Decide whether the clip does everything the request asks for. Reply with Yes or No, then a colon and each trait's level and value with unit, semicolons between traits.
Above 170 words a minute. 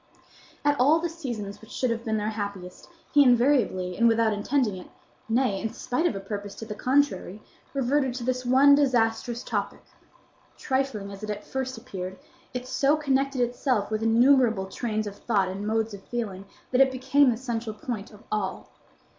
Yes: average, 180 wpm